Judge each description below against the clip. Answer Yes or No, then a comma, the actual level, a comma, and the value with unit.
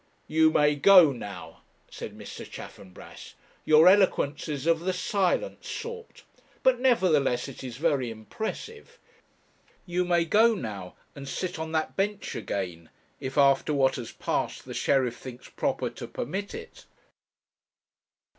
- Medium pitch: Yes, medium, 155 Hz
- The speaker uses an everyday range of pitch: No, wide, 6.4 semitones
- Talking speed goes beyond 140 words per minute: No, slow, 135 wpm